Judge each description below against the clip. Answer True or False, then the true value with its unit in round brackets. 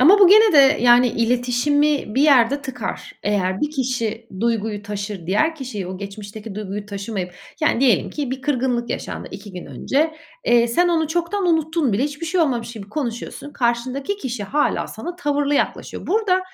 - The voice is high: True (250 Hz)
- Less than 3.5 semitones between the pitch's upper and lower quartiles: False (5.6 semitones)